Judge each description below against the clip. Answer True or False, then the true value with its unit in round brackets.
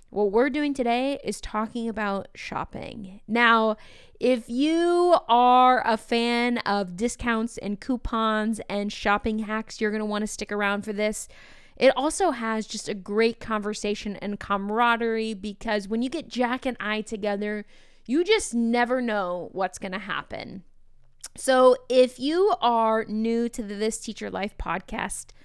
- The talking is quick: False (155 wpm)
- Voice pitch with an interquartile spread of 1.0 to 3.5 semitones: True (2.7 semitones)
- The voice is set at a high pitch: True (225 Hz)